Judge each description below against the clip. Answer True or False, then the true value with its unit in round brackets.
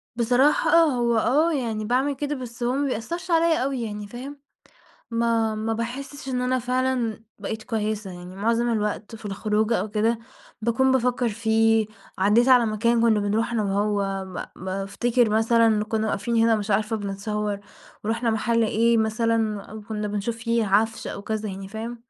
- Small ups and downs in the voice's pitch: True (2.2 semitones)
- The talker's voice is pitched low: False (225 Hz)